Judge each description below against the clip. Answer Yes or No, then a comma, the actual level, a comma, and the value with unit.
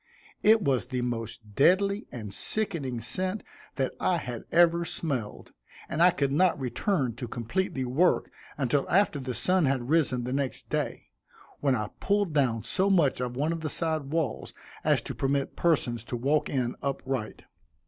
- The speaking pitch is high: No, medium, 140 Hz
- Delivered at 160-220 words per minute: Yes, average, 170 wpm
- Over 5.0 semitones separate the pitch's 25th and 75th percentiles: Yes, wide, 5.5 semitones